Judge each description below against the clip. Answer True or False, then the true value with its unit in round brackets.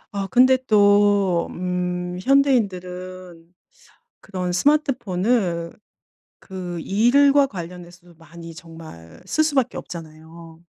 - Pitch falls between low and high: True (180 Hz)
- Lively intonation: False (4.3 semitones)